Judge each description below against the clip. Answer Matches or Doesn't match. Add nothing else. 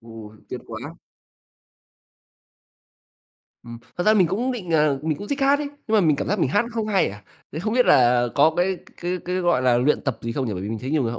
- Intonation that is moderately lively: Doesn't match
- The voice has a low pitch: Doesn't match